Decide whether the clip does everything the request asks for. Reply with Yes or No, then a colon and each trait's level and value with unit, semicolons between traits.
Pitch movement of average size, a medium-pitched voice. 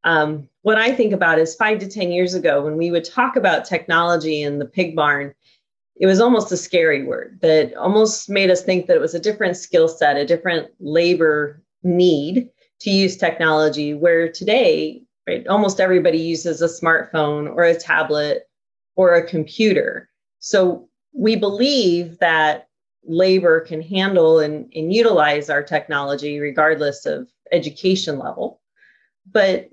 Yes: average, 3.9 semitones; medium, 170 Hz